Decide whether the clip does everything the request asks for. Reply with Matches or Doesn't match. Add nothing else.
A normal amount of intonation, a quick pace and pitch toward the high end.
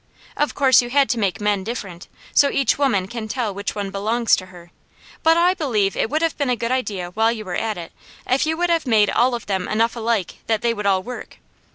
Matches